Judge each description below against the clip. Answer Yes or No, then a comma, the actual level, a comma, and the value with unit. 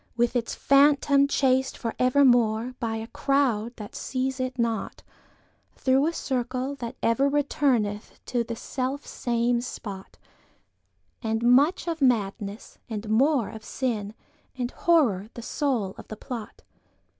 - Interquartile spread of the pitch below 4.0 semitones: Yes, average, 3.5 semitones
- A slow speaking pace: Yes, slow, 120 wpm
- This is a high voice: Yes, high, 245 Hz